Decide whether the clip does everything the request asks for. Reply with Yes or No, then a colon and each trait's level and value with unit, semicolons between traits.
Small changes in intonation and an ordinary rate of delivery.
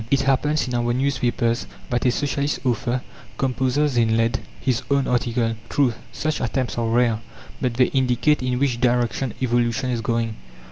Yes: narrow, 2.2 semitones; average, 160 wpm